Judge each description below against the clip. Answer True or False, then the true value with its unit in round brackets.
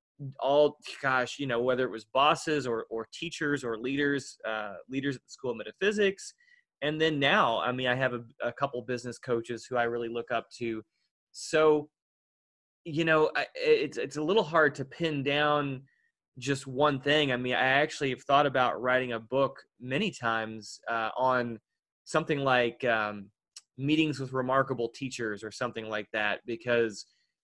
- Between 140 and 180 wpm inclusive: True (175 wpm)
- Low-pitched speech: True (130 Hz)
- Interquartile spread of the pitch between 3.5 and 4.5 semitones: True (4.0 semitones)